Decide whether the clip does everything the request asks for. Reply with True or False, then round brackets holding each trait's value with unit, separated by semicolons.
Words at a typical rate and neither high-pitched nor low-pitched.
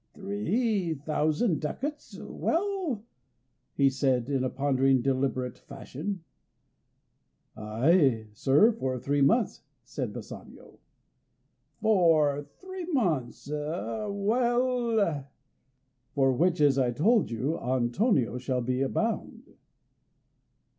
False (95 wpm; 150 Hz)